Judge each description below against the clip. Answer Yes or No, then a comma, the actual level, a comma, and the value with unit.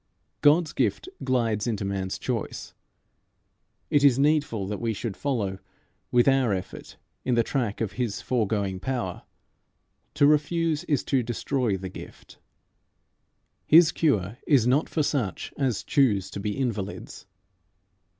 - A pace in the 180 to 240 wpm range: No, slow, 135 wpm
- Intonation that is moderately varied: No, wide, 5.7 semitones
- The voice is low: Yes, low, 120 Hz